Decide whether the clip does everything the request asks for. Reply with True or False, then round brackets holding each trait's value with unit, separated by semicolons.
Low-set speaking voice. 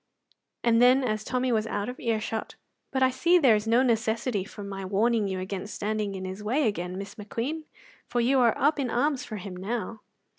False (225 Hz)